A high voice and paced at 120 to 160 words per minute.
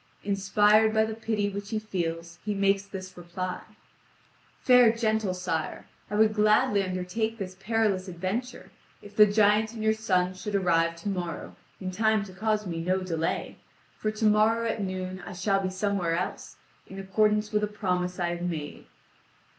No: high, 200 Hz; average, 170 wpm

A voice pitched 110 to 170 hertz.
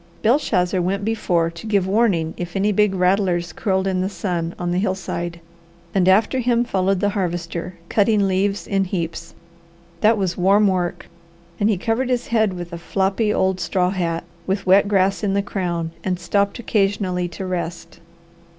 No: high, 190 Hz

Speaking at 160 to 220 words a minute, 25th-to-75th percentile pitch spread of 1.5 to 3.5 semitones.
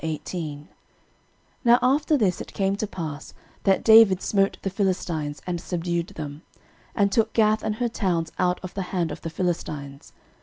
No: average, 165 wpm; average, 4.2 semitones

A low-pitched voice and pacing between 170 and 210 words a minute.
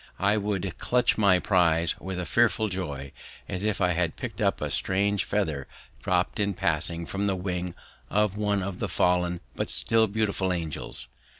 Yes: very low, 95 Hz; average, 175 wpm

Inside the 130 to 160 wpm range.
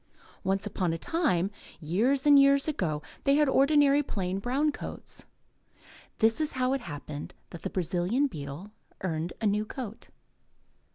Yes: average, 150 wpm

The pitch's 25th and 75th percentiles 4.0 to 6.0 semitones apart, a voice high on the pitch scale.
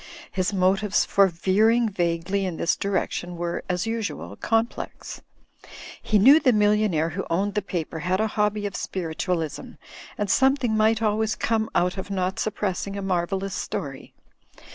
No: average, 3.1 semitones; high, 195 Hz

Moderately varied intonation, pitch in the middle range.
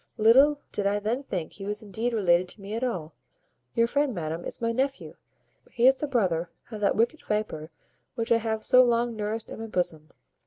No: average, 3.5 semitones; high, 220 Hz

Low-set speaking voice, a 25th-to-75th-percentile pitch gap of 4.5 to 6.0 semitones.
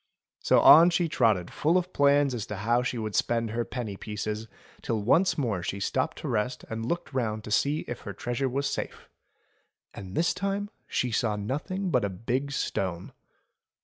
Yes: low, 120 Hz; average, 5.1 semitones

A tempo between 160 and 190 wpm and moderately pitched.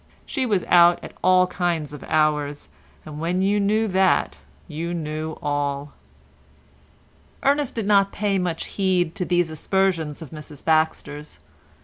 No: average, 140 wpm; medium, 170 Hz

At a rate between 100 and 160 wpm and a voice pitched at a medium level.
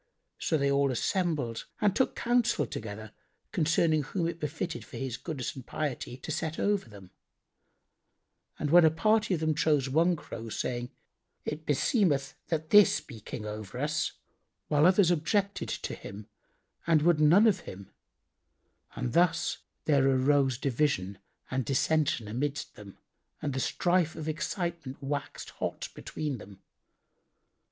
Yes: average, 145 wpm; medium, 150 Hz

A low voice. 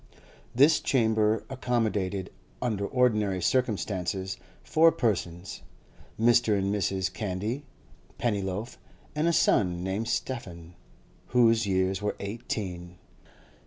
Yes: low, 105 Hz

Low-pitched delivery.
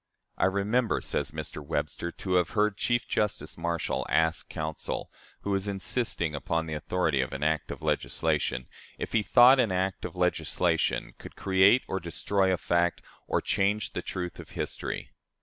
Yes: very low, 90 Hz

